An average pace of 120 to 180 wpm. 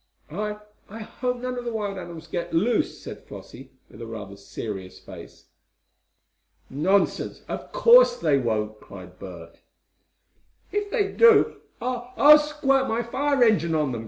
Yes: average, 150 wpm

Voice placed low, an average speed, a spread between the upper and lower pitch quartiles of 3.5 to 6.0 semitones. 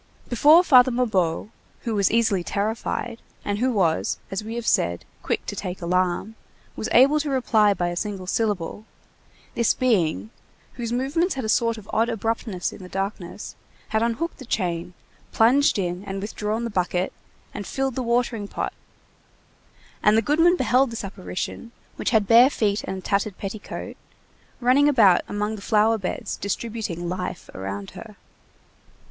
No: high, 215 Hz; average, 160 wpm; average, 4.1 semitones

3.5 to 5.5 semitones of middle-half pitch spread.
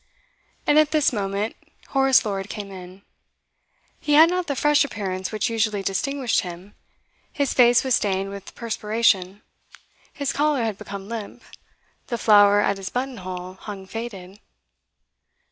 Yes: average, 5.0 semitones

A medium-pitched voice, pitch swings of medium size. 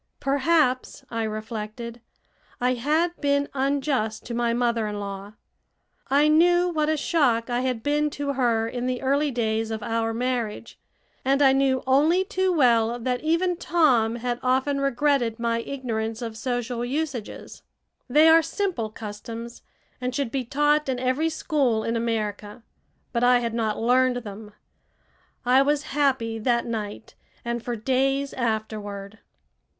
No: very high, 250 Hz; average, 3.8 semitones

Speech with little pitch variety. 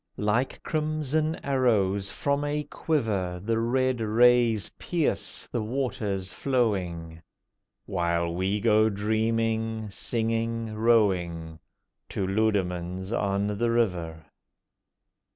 No: average, 3.9 semitones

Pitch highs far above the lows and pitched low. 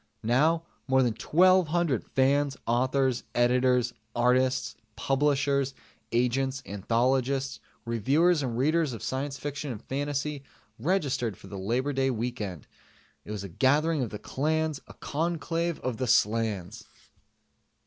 No: average, 3.3 semitones; low, 130 Hz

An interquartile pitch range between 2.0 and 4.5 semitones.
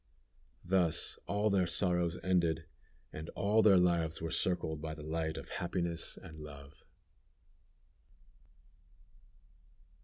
Yes: narrow, 2.5 semitones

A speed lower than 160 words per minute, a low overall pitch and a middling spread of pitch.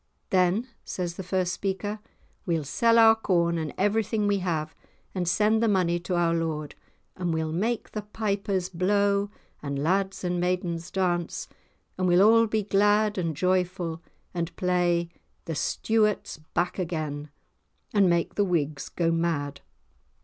No: average, 150 wpm; medium, 180 Hz; average, 3.3 semitones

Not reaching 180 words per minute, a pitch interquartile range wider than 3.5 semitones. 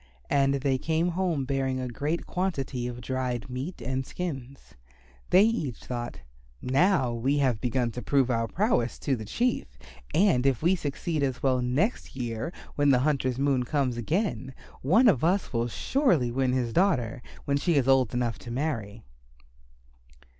Yes: average, 165 wpm; average, 4.3 semitones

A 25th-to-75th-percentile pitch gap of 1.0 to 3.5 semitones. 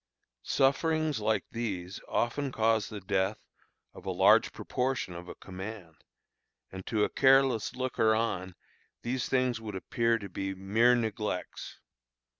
No: average, 4.3 semitones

